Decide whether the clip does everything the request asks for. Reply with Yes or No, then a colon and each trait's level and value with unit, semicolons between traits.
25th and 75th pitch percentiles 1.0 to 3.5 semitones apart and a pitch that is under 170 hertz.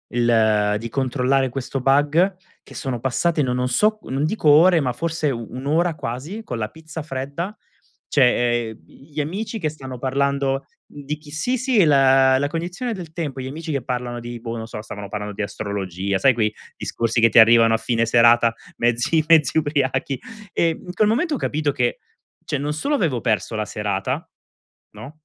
No: average, 4.9 semitones; low, 135 Hz